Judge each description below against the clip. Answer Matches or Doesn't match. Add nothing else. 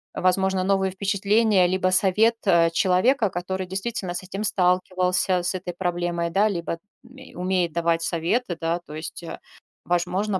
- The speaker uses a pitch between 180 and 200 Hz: Matches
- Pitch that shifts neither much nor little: Doesn't match